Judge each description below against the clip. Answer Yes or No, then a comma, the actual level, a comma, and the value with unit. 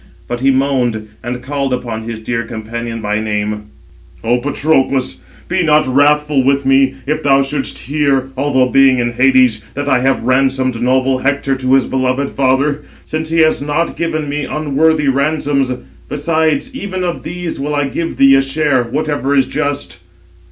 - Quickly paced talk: No, average, 165 wpm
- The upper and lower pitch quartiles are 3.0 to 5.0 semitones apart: No, narrow, 2.5 semitones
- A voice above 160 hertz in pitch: No, low, 135 Hz